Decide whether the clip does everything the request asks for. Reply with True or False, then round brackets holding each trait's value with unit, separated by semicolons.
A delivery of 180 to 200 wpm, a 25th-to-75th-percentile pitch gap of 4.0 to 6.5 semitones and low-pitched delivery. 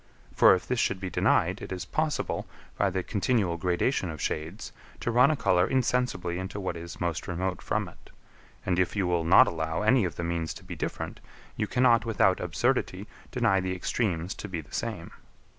True (195 wpm; 4.3 semitones; 95 Hz)